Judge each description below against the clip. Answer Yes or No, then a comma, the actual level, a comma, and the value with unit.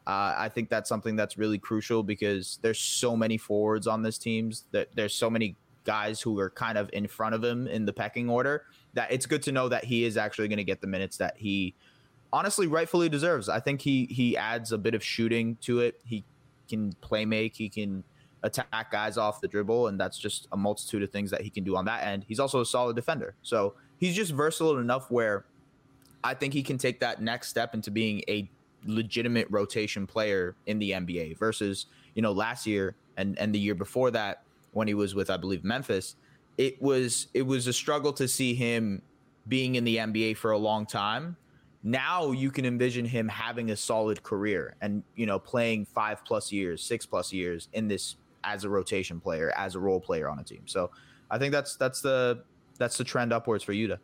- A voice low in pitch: Yes, low, 110 Hz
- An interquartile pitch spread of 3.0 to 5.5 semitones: Yes, average, 3.3 semitones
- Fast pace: Yes, fast, 220 wpm